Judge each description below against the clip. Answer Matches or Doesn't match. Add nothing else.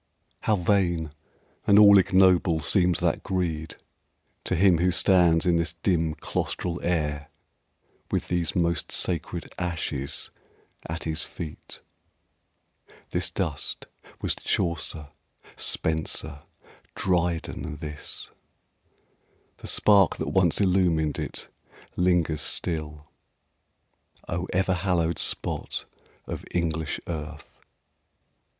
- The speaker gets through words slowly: Matches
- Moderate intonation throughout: Doesn't match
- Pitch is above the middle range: Doesn't match